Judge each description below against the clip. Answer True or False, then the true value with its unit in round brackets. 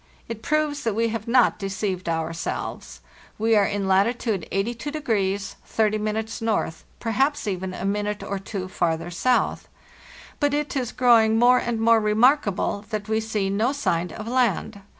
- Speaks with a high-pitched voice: True (215 Hz)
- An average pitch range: True (3.3 semitones)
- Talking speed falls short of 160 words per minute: True (150 wpm)